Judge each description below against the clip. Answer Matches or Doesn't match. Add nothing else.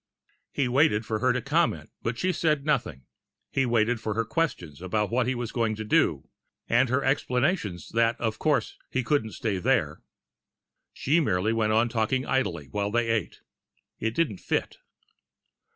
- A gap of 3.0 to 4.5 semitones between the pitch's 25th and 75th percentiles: Matches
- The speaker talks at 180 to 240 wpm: Doesn't match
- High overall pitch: Doesn't match